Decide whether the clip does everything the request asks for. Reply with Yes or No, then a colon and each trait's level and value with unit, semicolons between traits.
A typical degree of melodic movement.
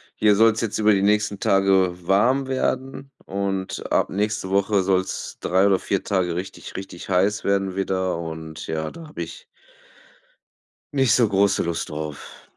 No: narrow, 2.3 semitones